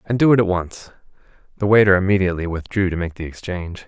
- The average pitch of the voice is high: No, very low, 95 Hz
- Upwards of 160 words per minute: Yes, average, 200 wpm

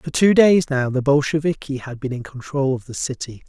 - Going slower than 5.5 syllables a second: Yes, 5.3 syllables/s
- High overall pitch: No, medium, 140 Hz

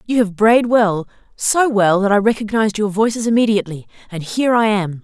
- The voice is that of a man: No, female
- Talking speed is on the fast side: No, average, 190 wpm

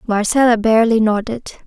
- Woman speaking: Yes, female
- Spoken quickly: No, slow, 110 wpm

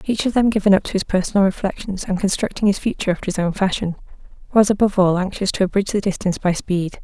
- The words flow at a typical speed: No, fast, 230 wpm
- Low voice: No, high, 195 Hz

